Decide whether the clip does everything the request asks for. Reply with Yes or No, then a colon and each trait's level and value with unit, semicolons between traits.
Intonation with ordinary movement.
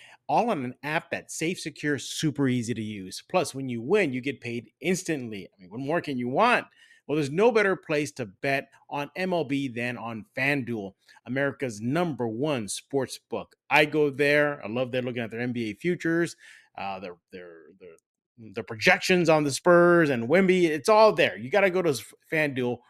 No: wide, 5.8 semitones